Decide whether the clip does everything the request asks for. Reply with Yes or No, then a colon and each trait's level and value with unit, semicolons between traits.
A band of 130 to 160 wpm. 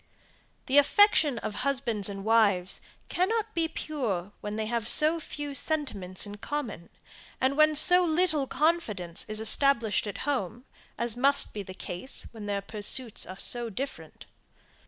Yes: average, 150 wpm